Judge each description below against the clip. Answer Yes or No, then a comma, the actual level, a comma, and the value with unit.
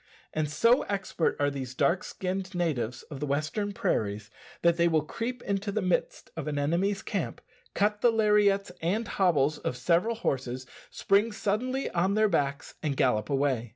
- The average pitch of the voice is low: No, medium, 170 Hz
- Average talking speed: Yes, average, 170 wpm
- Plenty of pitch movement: Yes, wide, 6.3 semitones